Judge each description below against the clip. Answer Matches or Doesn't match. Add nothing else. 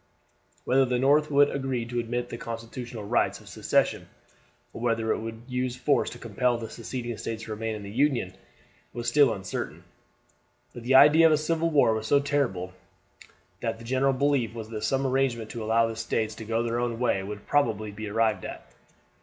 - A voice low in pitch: Matches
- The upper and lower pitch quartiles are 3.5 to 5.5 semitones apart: Doesn't match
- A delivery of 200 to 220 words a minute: Matches